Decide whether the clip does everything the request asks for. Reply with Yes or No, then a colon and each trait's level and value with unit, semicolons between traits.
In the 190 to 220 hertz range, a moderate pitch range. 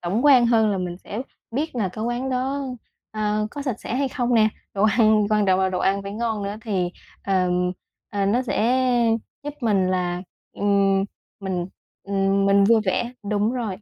Yes: high, 210 Hz; average, 3.4 semitones